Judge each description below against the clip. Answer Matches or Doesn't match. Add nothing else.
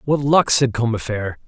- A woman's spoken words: Doesn't match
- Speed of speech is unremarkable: Matches